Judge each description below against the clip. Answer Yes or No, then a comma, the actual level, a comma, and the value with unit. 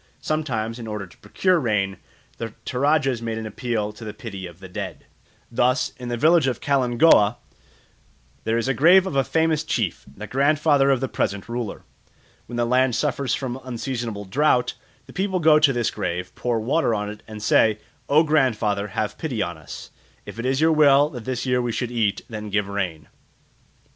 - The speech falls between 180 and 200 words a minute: Yes, average, 190 wpm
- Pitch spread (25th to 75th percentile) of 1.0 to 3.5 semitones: No, average, 4.7 semitones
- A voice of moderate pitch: No, low, 120 Hz